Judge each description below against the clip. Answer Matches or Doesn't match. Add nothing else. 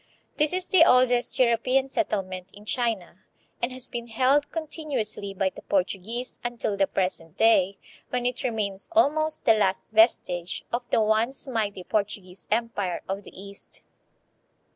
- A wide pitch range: Doesn't match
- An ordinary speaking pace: Matches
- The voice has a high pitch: Matches